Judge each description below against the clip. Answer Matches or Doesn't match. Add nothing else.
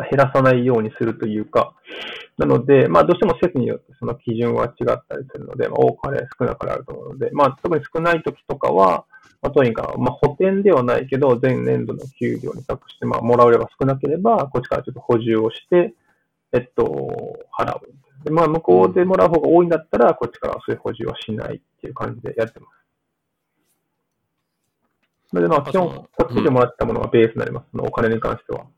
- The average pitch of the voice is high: Doesn't match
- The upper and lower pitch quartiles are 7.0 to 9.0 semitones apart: Doesn't match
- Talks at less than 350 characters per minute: Doesn't match